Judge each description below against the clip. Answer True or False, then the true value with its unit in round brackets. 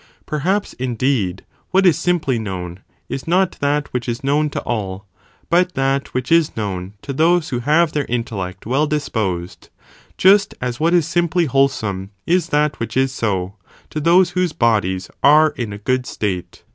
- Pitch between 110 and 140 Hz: True (135 Hz)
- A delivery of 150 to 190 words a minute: True (175 wpm)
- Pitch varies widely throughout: True (6.9 semitones)